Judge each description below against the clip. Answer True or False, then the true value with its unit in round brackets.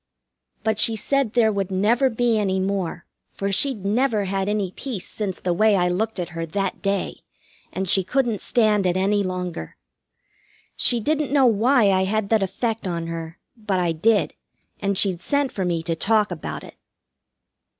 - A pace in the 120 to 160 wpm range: False (180 wpm)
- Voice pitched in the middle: False (200 Hz)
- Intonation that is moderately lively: True (3.3 semitones)